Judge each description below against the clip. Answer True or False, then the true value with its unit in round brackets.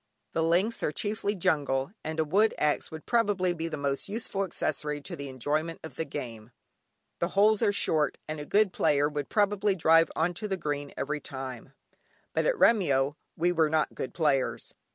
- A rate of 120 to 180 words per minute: False (190 wpm)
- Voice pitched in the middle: True (160 Hz)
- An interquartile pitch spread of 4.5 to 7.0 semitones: True (5.1 semitones)